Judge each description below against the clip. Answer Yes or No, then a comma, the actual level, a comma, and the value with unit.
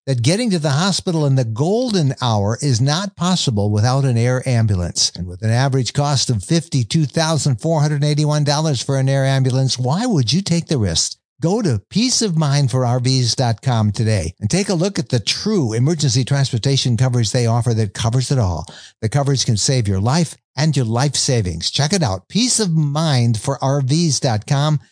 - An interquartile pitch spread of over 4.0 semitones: Yes, average, 4.6 semitones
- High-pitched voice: No, low, 135 Hz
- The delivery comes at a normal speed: Yes, average, 160 wpm